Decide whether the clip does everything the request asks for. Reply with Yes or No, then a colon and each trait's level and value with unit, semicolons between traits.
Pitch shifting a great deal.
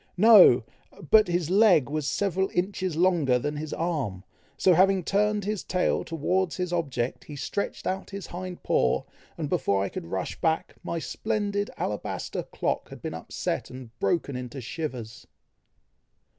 Yes: wide, 6.1 semitones